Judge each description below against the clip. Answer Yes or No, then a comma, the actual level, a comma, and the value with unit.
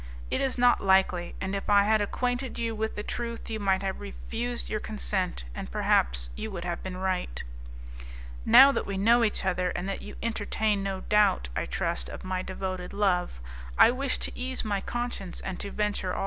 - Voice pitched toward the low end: No, high, 200 Hz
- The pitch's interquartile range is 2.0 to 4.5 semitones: Yes, average, 3.3 semitones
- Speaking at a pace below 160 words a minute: No, average, 200 wpm